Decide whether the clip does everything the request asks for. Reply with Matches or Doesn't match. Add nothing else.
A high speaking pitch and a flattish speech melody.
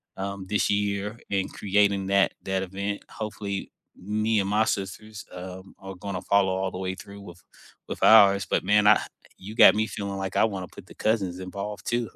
Doesn't match